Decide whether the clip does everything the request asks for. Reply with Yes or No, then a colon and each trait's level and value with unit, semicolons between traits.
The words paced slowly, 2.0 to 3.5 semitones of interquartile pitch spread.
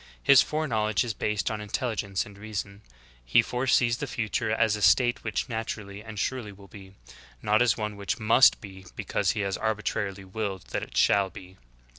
No: average, 180 wpm; narrow, 2.5 semitones